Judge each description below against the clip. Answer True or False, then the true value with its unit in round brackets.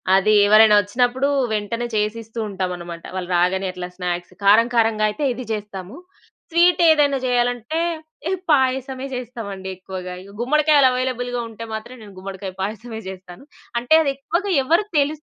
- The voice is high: True (225 Hz)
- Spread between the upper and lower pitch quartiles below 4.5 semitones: False (5.2 semitones)